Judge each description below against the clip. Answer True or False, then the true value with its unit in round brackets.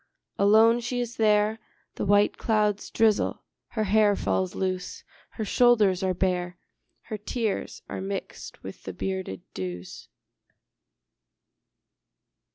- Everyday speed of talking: False (115 wpm)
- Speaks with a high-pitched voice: True (205 Hz)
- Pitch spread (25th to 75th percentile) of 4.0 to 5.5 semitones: False (2.9 semitones)